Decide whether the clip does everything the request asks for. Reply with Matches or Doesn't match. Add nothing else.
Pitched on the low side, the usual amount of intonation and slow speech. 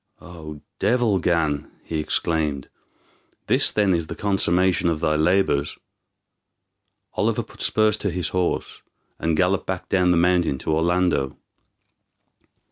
Matches